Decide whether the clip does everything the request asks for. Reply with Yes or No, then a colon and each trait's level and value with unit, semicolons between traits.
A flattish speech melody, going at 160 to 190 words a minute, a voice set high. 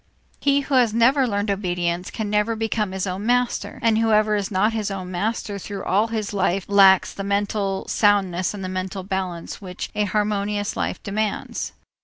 Yes: narrow, 2.2 semitones; average, 175 wpm; high, 205 Hz